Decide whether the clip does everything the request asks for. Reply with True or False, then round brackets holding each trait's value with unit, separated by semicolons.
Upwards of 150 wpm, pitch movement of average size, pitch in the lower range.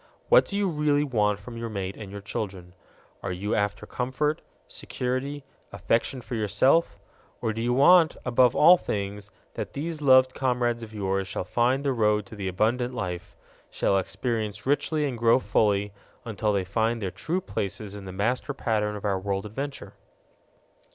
True (170 wpm; 4.4 semitones; 115 Hz)